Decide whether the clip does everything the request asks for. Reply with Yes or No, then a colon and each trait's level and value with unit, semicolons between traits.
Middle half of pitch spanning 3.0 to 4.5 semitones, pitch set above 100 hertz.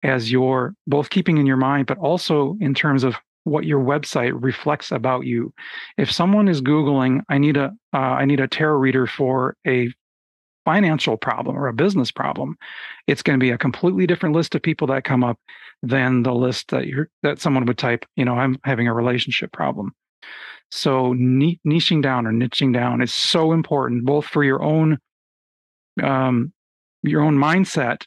Yes: average, 3.3 semitones; low, 135 Hz